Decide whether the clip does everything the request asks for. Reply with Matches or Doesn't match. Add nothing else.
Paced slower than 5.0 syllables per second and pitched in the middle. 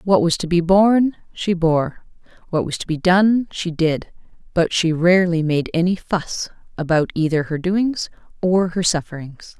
Matches